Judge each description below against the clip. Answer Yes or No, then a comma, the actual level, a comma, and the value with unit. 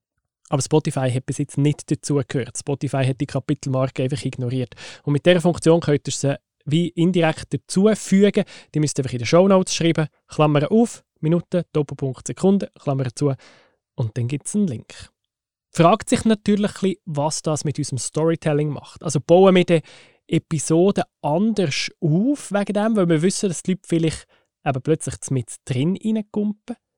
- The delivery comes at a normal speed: Yes, average, 165 wpm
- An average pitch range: Yes, average, 4.6 semitones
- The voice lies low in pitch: No, medium, 155 Hz